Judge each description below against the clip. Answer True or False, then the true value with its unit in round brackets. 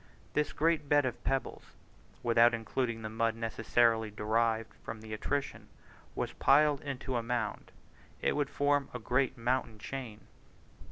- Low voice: True (120 Hz)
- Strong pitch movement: False (3.4 semitones)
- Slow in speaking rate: False (150 wpm)